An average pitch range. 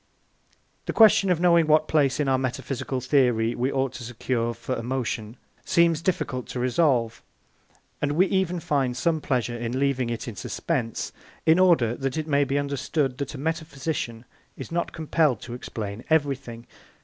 Yes: average, 4.6 semitones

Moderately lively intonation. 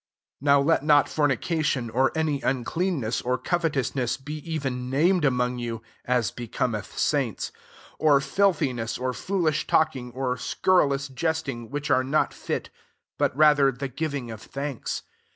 Yes: average, 3.6 semitones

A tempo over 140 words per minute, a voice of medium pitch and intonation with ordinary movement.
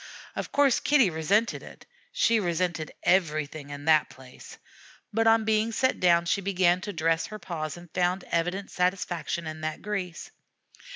Yes: average, 160 wpm; medium, 180 Hz; average, 4.3 semitones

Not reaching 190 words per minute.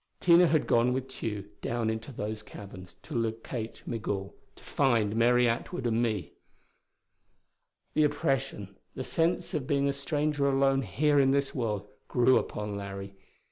Yes: average, 150 wpm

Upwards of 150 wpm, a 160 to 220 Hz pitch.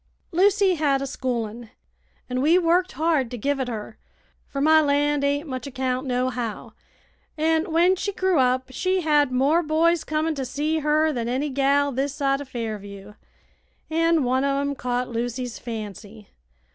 No: average, 165 wpm; very high, 275 Hz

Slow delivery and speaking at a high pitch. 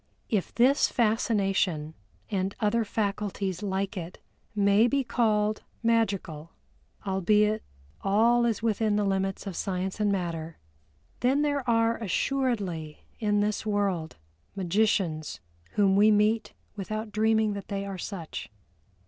Yes: slow, 125 wpm; high, 205 Hz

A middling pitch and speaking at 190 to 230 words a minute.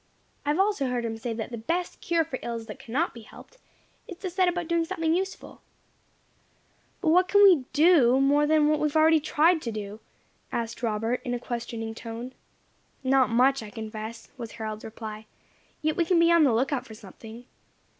No: very high, 260 Hz; average, 195 wpm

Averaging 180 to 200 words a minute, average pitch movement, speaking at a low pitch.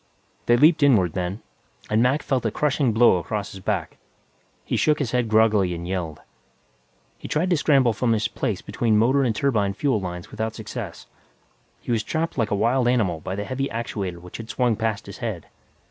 Yes: average, 195 wpm; average, 4.3 semitones; low, 110 Hz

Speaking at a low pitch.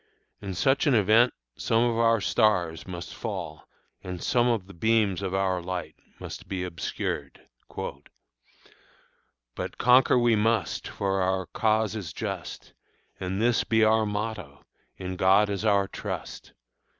Yes: low, 100 Hz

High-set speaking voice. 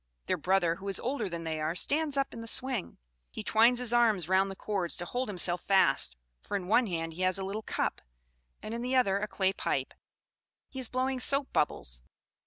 Yes: high, 200 Hz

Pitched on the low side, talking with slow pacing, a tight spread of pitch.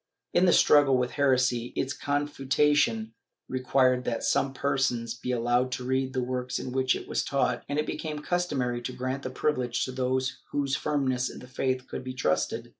No: low, 130 Hz; average, 190 wpm; narrow, 1.8 semitones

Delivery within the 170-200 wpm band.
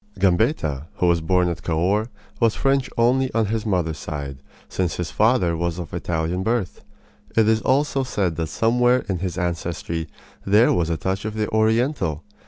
Yes: average, 175 wpm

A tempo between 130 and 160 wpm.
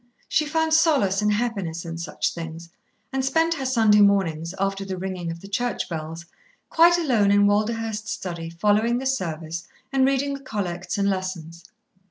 No: average, 170 wpm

